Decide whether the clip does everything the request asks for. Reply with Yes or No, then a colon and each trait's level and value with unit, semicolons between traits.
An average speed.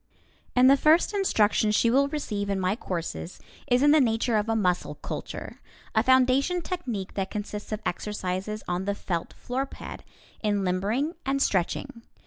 Yes: average, 160 wpm